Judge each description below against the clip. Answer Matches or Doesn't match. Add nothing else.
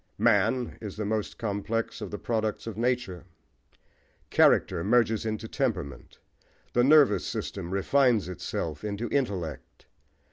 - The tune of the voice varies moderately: Matches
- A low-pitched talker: Matches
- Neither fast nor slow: Doesn't match